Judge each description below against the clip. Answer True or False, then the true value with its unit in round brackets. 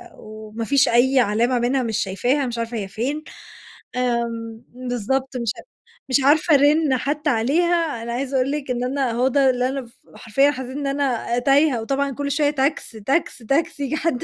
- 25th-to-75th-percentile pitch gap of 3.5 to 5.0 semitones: False (3.1 semitones)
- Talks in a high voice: True (260 Hz)